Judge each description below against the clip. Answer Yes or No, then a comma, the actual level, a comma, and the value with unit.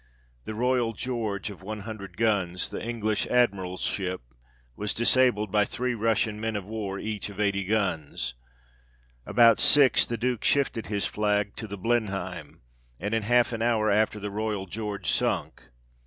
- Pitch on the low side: Yes, low, 105 Hz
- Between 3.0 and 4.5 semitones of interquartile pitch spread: No, narrow, 2.5 semitones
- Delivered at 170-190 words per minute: No, average, 155 wpm